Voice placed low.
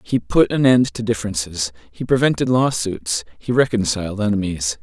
Yes: low, 105 Hz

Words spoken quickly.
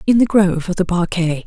Yes: fast, 245 wpm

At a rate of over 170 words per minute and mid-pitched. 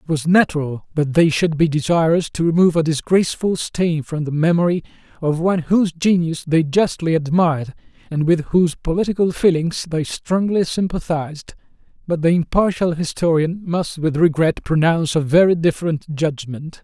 No: average, 155 wpm; medium, 165 Hz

